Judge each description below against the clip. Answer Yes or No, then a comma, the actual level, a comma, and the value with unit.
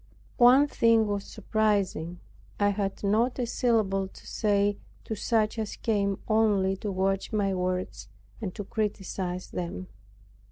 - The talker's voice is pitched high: Yes, high, 205 Hz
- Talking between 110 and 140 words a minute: Yes, slow, 135 wpm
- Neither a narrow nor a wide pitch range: No, narrow, 2.3 semitones